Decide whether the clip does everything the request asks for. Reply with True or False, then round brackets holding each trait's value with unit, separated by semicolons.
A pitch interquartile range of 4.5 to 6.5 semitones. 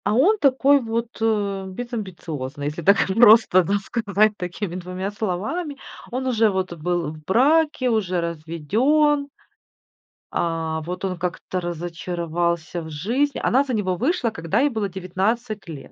True (5.5 semitones)